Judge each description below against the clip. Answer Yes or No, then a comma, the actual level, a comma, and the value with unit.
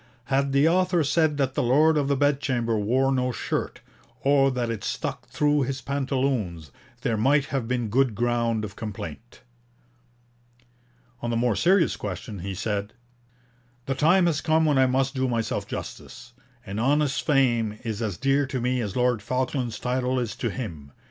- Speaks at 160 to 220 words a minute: Yes, average, 170 wpm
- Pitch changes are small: No, average, 3.5 semitones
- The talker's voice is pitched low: Yes, low, 130 Hz